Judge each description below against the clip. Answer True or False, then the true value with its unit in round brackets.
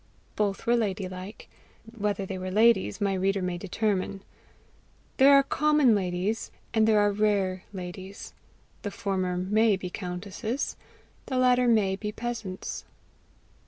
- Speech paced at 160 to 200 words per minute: False (135 wpm)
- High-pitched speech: True (200 Hz)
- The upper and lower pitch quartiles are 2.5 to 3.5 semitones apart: True (3.0 semitones)